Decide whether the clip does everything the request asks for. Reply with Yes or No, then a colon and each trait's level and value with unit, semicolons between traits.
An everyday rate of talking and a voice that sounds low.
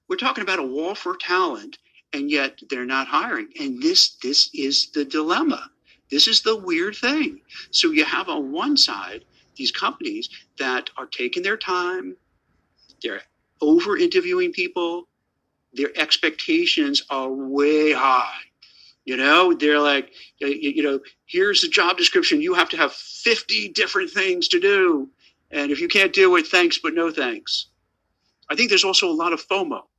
No: average, 160 wpm; very high, 270 Hz